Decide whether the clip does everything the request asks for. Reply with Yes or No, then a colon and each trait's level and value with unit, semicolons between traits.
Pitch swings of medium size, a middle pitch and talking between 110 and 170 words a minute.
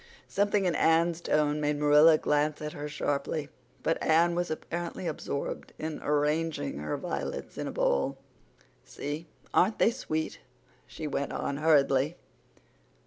No: narrow, 2.0 semitones; medium, 155 Hz; average, 140 wpm